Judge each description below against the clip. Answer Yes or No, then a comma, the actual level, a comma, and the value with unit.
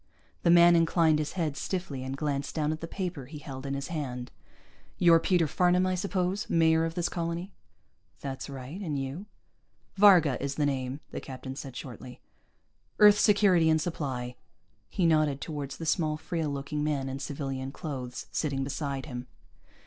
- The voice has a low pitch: No, medium, 150 Hz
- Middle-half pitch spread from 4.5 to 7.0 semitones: No, average, 3.8 semitones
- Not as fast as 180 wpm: Yes, average, 170 wpm